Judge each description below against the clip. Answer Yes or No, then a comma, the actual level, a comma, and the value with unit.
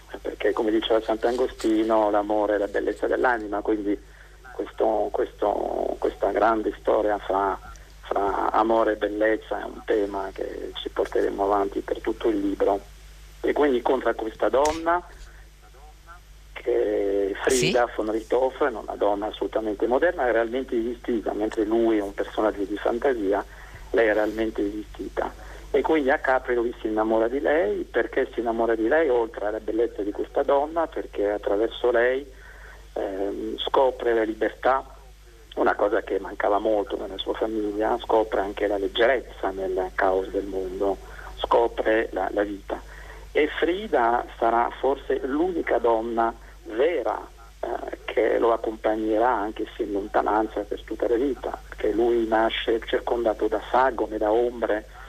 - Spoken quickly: No, average, 145 wpm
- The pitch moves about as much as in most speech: No, wide, 6.5 semitones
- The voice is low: Yes, low, 115 Hz